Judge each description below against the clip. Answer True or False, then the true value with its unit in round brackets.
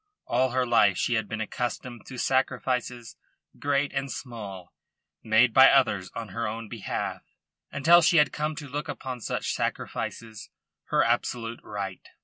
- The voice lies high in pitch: False (120 Hz)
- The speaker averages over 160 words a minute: False (150 wpm)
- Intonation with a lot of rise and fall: False (3.3 semitones)